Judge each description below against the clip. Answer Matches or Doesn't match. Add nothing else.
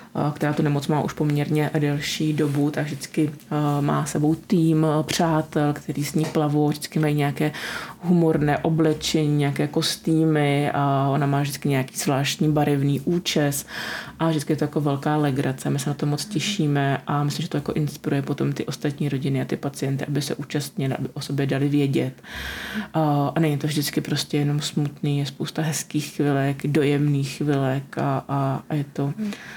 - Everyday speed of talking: Doesn't match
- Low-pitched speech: Doesn't match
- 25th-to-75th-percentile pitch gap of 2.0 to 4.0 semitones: Doesn't match